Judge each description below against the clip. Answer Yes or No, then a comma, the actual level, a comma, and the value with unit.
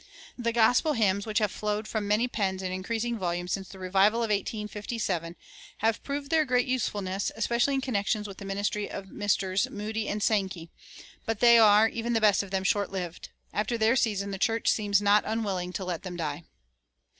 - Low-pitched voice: No, high, 210 Hz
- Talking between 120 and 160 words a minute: No, average, 190 wpm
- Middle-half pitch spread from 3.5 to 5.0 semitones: No, average, 2.9 semitones